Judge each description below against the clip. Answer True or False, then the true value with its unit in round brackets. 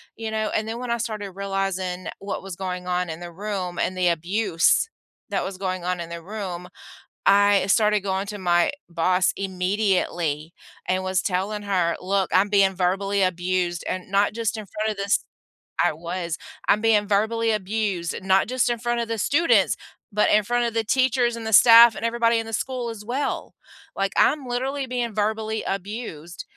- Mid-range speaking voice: False (200 Hz)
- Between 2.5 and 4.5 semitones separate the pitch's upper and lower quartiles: True (3.5 semitones)